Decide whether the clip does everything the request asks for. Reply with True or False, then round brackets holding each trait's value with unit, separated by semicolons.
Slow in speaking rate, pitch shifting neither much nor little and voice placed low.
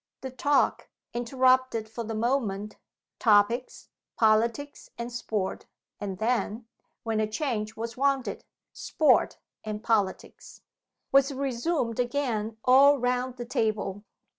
False (115 wpm; 3.1 semitones; 235 Hz)